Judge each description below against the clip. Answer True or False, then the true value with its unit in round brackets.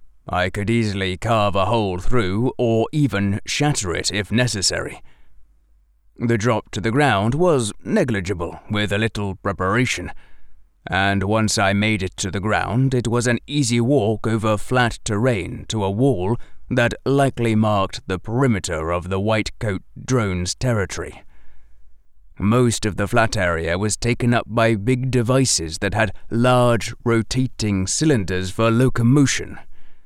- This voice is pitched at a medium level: False (110 Hz)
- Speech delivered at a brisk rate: False (145 wpm)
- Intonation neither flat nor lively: True (4.0 semitones)